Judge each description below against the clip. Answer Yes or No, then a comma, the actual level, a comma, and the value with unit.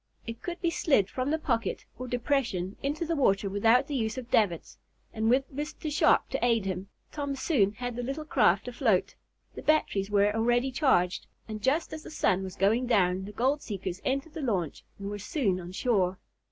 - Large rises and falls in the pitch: Yes, wide, 5.7 semitones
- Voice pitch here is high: Yes, high, 235 Hz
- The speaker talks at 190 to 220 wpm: Yes, average, 200 wpm